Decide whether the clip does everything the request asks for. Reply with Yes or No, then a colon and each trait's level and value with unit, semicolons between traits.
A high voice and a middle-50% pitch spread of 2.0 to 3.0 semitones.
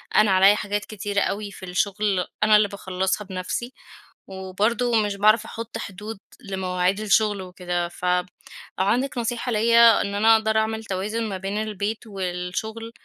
Yes: high, 205 Hz; narrow, 2.6 semitones